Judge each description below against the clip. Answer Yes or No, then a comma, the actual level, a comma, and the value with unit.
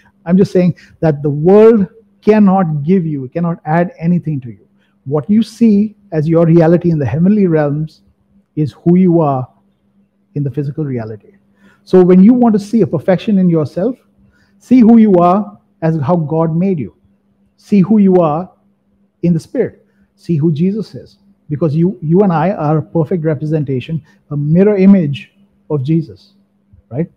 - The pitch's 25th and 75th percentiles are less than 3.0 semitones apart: No, average, 4.5 semitones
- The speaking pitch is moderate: Yes, medium, 175 Hz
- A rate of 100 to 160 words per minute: No, average, 170 wpm